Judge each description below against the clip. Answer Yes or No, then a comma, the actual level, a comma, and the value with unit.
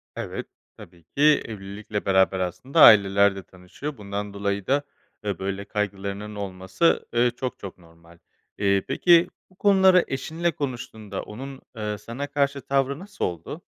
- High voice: No, low, 105 Hz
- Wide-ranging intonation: Yes, wide, 6.0 semitones